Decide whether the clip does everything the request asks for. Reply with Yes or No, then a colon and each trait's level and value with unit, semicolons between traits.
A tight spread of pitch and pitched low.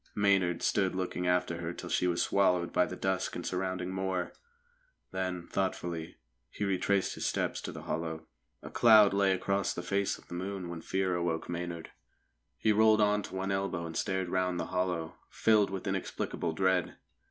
Yes: narrow, 2.0 semitones; very low, 95 Hz